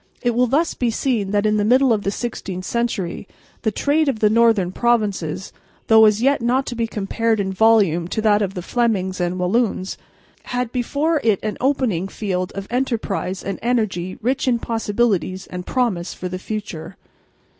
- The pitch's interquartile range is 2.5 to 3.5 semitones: No, average, 4.1 semitones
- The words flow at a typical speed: Yes, average, 180 wpm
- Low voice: No, high, 215 Hz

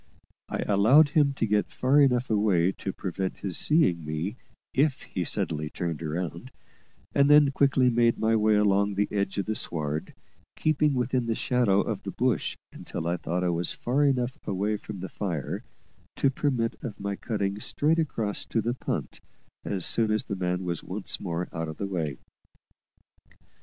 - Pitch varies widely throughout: Yes, wide, 5.7 semitones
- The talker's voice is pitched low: Yes, low, 105 Hz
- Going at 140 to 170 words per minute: No, average, 180 wpm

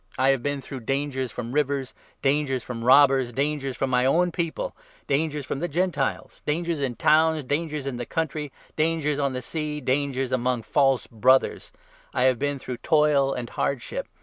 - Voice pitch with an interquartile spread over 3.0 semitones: No, narrow, 2.6 semitones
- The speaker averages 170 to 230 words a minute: Yes, average, 175 wpm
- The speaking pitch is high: No, medium, 140 Hz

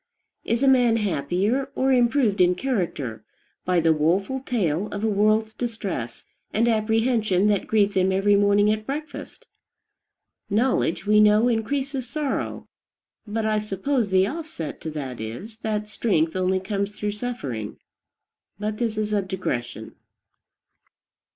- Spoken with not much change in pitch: No, average, 3.8 semitones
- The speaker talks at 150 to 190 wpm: No, average, 140 wpm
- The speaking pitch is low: No, high, 210 Hz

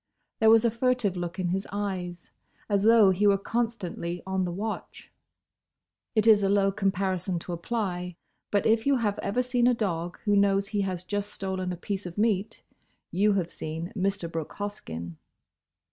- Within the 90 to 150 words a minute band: No, average, 175 wpm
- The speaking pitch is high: Yes, high, 195 Hz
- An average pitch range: Yes, average, 3.0 semitones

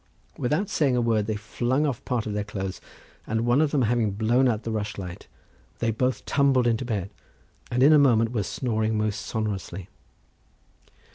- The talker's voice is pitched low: Yes, low, 115 Hz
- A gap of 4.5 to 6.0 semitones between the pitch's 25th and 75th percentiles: No, average, 3.1 semitones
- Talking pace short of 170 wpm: No, average, 180 wpm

